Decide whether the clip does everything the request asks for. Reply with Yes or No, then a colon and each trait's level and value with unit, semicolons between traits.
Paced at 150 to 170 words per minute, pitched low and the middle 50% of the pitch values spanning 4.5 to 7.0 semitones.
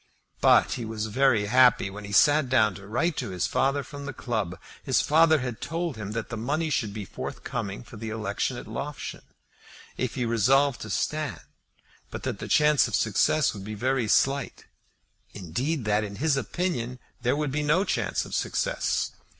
No: average, 185 wpm; low, 125 Hz; average, 5.2 semitones